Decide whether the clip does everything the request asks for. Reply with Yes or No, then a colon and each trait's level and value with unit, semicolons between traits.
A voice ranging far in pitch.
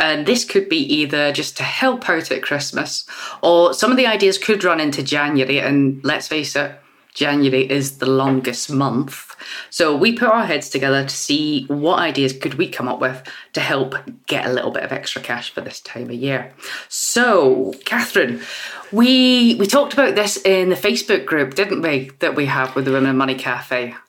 Yes: wide, 7.2 semitones